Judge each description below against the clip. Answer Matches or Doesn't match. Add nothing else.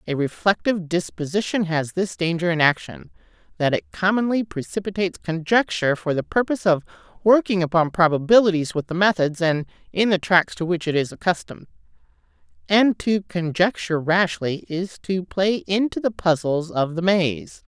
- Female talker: Matches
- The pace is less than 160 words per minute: Matches